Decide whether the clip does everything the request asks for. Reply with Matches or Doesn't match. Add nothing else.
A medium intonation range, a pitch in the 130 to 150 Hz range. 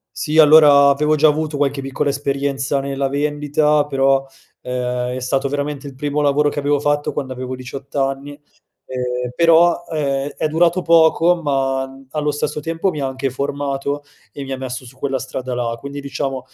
Doesn't match